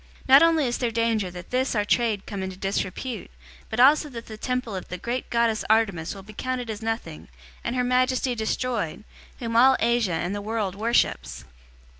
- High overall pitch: Yes, high, 230 Hz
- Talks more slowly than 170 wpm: No, average, 195 wpm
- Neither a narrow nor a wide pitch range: Yes, average, 3.8 semitones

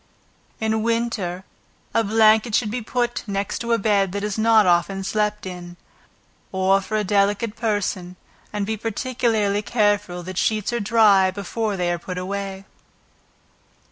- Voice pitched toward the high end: Yes, high, 205 Hz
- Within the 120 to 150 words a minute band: Yes, average, 145 wpm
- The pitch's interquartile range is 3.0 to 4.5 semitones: No, narrow, 2.5 semitones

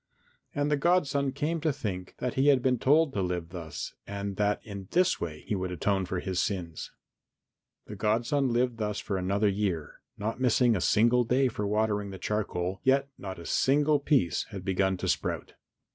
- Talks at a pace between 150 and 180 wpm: No, average, 190 wpm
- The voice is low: Yes, low, 105 Hz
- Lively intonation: Yes, wide, 5.7 semitones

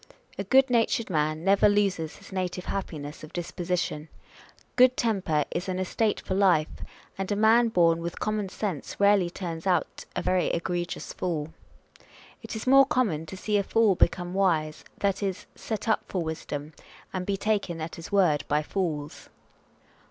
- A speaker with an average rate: Yes, average, 165 wpm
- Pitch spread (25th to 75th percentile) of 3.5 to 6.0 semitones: Yes, average, 3.9 semitones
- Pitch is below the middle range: No, medium, 185 Hz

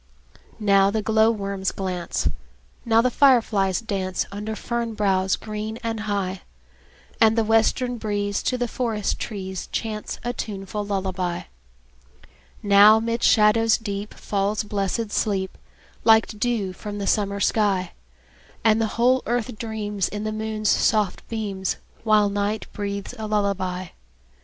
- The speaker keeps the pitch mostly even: Yes, narrow, 2.0 semitones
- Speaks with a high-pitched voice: Yes, high, 210 Hz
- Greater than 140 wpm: No, slow, 135 wpm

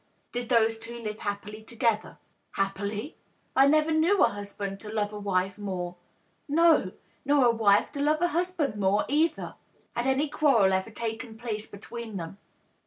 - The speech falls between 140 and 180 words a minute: No, average, 190 wpm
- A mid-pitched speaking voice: No, high, 225 Hz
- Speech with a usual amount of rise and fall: No, wide, 5.7 semitones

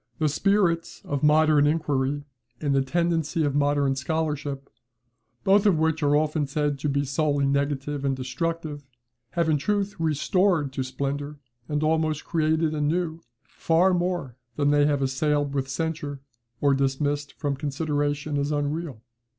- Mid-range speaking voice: Yes, medium, 145 Hz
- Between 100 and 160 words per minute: Yes, average, 145 wpm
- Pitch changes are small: Yes, narrow, 2.2 semitones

